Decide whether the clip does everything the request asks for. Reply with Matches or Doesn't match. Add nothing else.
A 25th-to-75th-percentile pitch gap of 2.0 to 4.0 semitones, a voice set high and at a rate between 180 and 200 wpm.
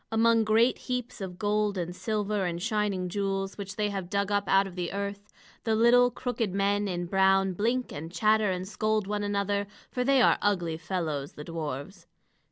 Matches